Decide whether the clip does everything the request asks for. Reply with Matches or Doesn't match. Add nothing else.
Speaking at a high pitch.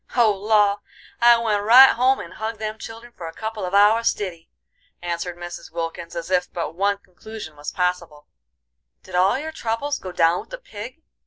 Matches